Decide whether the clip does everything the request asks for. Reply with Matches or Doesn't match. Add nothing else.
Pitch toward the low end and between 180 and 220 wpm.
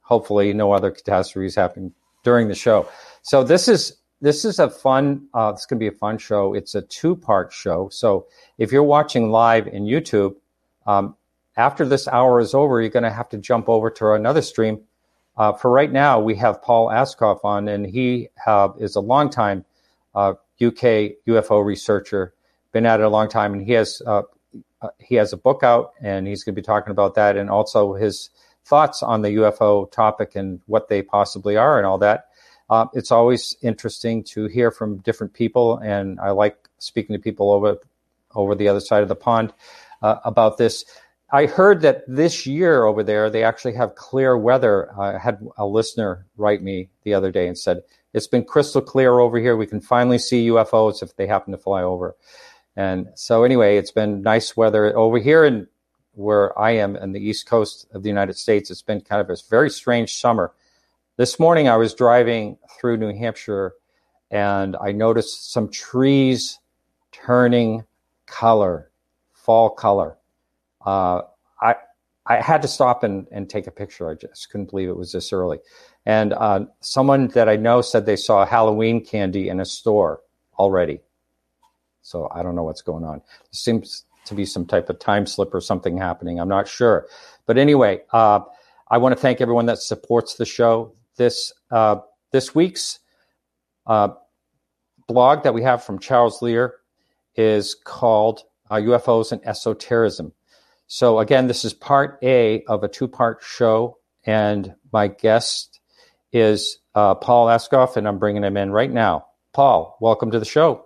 Matches